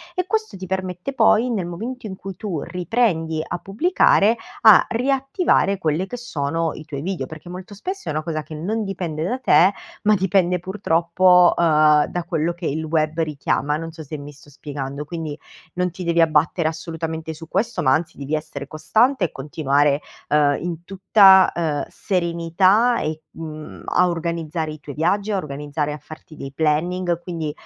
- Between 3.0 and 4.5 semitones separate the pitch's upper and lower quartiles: Yes, average, 3.7 semitones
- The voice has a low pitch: No, medium, 170 Hz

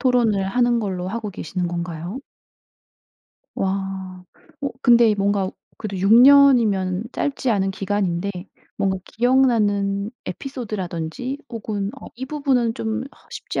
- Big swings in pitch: No, average, 4.2 semitones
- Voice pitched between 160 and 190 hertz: No, high, 205 Hz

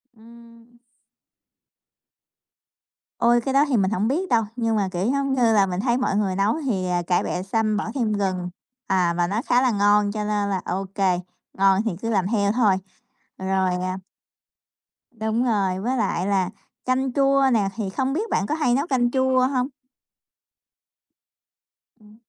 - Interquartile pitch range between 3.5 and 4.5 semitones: Yes, average, 4.2 semitones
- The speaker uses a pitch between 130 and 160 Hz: No, high, 215 Hz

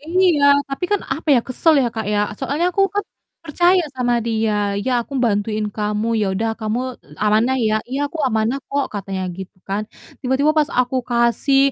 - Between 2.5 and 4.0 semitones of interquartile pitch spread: No, average, 4.9 semitones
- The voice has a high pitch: Yes, high, 245 Hz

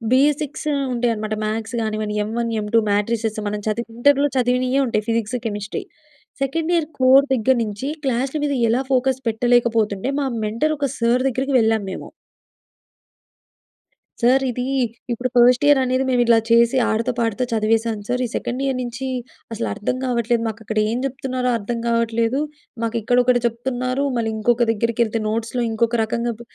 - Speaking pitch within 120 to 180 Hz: No, high, 235 Hz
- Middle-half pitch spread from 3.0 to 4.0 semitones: No, narrow, 2.4 semitones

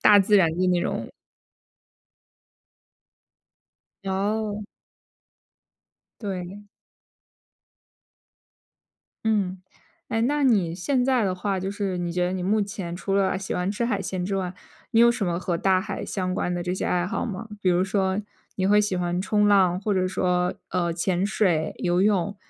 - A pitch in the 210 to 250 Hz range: No, high, 190 Hz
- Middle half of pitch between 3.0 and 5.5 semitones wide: No, narrow, 2.4 semitones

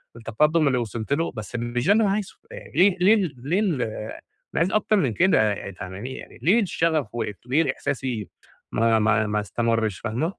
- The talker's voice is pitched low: Yes, low, 125 Hz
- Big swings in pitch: Yes, wide, 7.4 semitones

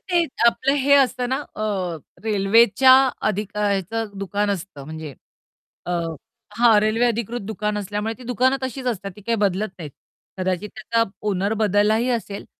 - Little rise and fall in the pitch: No, average, 3.0 semitones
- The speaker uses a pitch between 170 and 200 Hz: No, high, 215 Hz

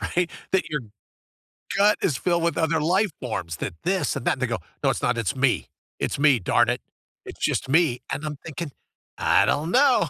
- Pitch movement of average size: No, wide, 5.7 semitones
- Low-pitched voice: No, medium, 150 Hz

